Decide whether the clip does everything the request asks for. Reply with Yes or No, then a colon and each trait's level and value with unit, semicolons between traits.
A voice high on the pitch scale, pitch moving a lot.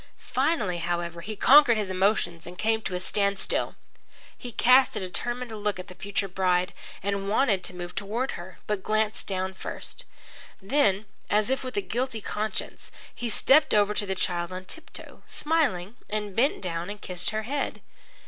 No: high, 205 Hz; average, 4.2 semitones